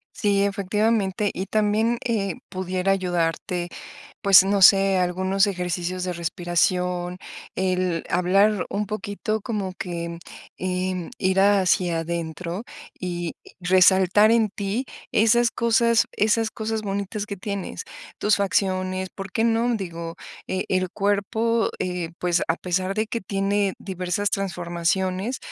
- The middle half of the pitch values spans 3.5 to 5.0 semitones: No, narrow, 2.4 semitones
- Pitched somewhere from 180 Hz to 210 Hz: Yes, high, 190 Hz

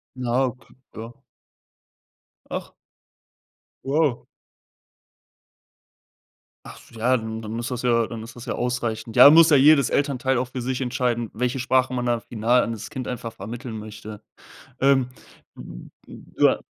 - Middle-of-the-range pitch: No, low, 120 Hz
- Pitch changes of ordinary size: No, narrow, 2.2 semitones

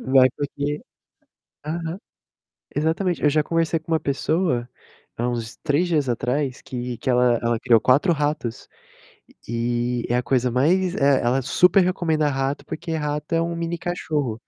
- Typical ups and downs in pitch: Yes, average, 5.0 semitones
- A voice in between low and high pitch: Yes, medium, 145 Hz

